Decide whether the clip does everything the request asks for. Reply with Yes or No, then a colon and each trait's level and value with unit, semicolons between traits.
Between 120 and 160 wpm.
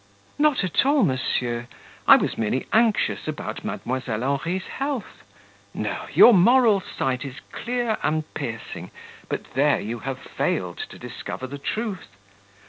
Yes: slow, 135 wpm